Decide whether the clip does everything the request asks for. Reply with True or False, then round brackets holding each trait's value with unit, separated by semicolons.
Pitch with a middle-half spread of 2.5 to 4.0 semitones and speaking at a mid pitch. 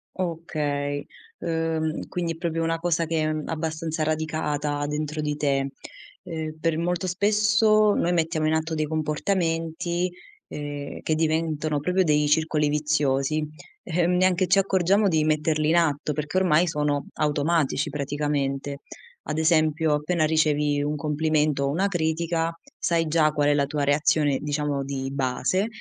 False (2.0 semitones; 155 Hz)